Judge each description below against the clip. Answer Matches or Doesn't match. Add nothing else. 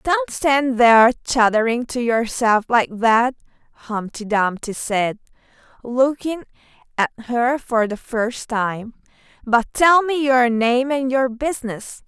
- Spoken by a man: Doesn't match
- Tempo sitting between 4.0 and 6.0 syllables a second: Doesn't match